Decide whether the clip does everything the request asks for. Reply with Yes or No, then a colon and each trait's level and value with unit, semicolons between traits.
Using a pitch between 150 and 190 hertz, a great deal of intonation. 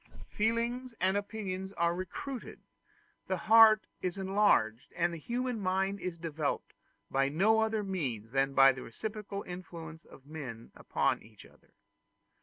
Yes: medium, 185 Hz; wide, 5.9 semitones